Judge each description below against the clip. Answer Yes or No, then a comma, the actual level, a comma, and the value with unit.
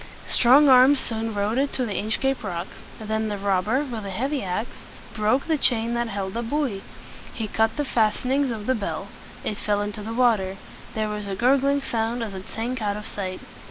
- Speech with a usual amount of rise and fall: Yes, average, 3.7 semitones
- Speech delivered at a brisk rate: Yes, fast, 215 wpm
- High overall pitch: Yes, high, 225 Hz